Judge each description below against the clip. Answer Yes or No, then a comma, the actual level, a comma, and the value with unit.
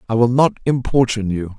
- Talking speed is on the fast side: No, average, 190 wpm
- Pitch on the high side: No, low, 115 Hz